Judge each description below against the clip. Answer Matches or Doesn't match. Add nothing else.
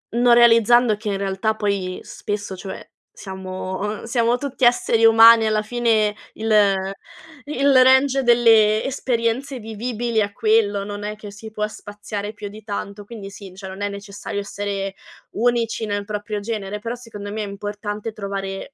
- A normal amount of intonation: Doesn't match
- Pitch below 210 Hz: Doesn't match